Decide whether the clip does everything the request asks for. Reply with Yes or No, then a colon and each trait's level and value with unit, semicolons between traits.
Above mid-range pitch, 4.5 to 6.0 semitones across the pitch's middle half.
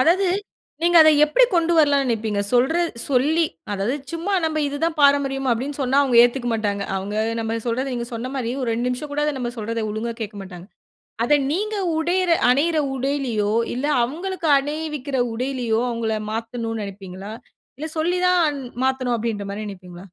Yes: very high, 255 Hz; average, 5.2 semitones